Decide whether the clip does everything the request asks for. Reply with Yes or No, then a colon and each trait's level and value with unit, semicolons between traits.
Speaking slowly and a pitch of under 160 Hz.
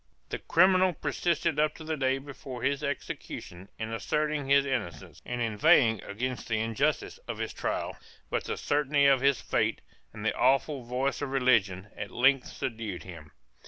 No: average, 165 wpm; low, 135 Hz